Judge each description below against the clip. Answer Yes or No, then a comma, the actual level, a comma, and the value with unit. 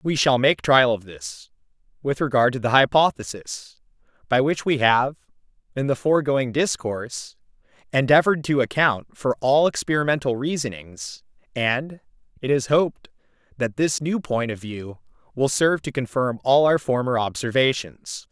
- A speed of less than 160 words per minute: Yes, average, 145 wpm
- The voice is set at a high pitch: No, low, 130 Hz